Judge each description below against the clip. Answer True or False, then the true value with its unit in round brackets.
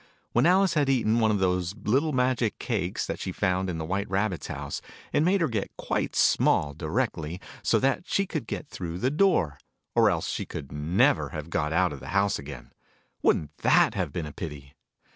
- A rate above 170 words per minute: True (200 wpm)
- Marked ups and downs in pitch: True (8.3 semitones)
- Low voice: True (95 Hz)